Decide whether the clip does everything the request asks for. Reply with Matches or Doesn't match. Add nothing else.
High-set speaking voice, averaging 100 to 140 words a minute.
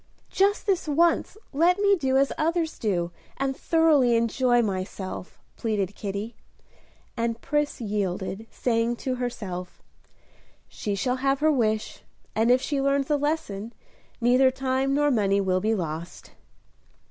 Matches